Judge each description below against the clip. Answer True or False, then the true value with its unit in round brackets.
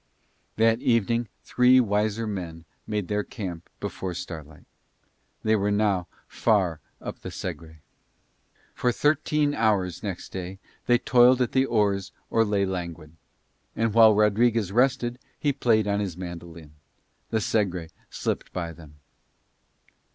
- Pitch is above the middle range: False (105 Hz)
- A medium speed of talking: False (130 wpm)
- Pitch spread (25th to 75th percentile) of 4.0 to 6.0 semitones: True (4.4 semitones)